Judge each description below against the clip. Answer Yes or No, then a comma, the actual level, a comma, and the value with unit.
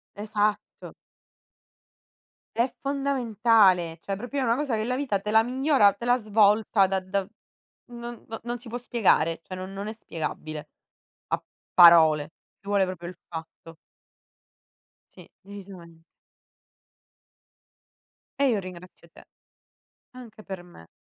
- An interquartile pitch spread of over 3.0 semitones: Yes, average, 4.6 semitones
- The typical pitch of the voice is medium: No, high, 205 Hz